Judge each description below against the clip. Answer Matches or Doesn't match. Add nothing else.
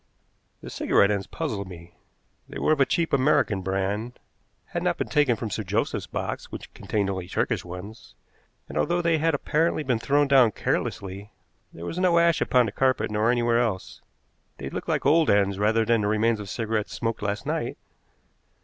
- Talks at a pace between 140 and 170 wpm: Doesn't match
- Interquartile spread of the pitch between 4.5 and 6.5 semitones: Matches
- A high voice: Doesn't match